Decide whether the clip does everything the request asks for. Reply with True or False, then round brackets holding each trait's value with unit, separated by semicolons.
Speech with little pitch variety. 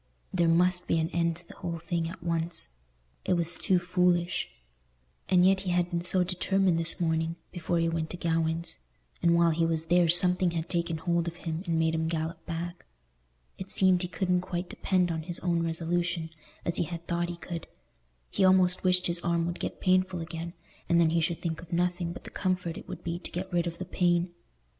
True (1.3 semitones)